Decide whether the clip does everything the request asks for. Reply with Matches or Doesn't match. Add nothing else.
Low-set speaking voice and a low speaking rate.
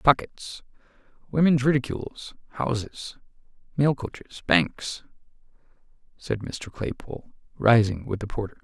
Matches